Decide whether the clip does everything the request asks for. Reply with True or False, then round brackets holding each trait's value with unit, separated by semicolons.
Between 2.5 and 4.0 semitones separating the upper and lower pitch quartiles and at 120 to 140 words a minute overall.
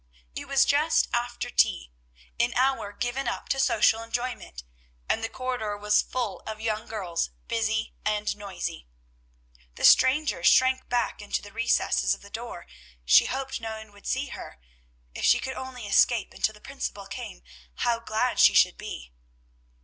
False (3.5 semitones; 165 wpm)